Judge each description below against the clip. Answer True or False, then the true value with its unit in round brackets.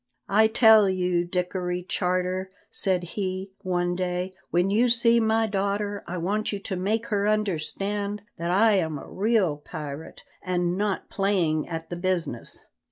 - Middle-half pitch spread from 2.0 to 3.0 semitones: True (2.7 semitones)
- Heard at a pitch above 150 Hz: True (185 Hz)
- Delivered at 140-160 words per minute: True (155 wpm)